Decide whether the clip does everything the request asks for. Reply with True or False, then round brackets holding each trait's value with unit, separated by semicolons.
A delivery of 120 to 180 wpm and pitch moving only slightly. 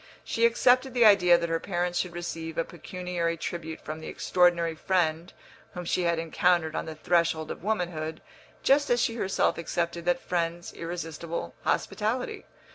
True (160 wpm; 1.7 semitones)